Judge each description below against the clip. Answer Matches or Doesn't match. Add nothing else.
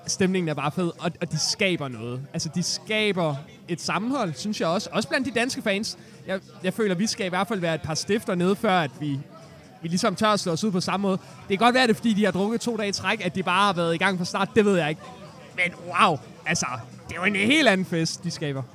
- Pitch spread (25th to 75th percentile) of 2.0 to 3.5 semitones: Doesn't match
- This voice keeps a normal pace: Doesn't match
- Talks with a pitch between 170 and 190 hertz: Matches